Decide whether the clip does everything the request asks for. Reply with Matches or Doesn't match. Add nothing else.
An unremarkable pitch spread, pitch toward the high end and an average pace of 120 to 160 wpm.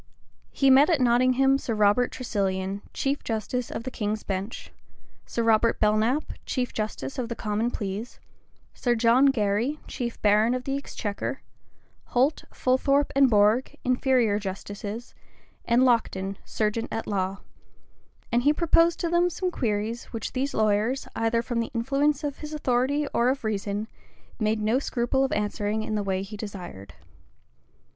Matches